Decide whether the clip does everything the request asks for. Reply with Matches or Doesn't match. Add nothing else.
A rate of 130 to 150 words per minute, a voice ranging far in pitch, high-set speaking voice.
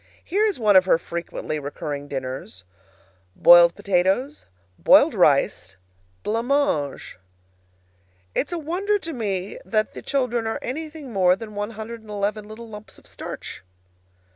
Matches